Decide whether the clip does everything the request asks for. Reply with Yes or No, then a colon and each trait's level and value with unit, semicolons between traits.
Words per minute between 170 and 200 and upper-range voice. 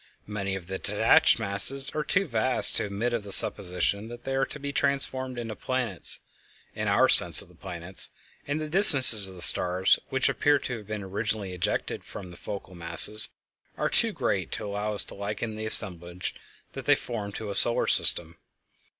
No: average, 190 wpm; low, 105 Hz